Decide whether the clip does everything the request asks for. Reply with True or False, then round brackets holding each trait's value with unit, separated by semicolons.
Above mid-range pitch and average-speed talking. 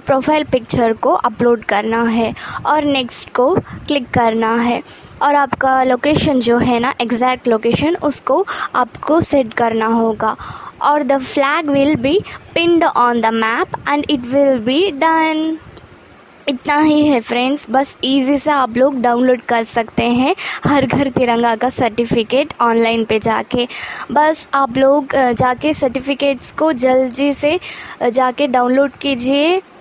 True (265 Hz; 145 wpm)